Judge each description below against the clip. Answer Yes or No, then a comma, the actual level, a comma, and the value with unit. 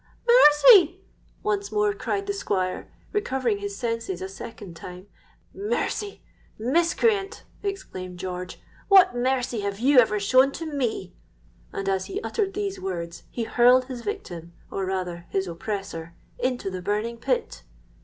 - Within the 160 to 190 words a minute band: No, slow, 135 wpm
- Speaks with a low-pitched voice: No, high, 230 Hz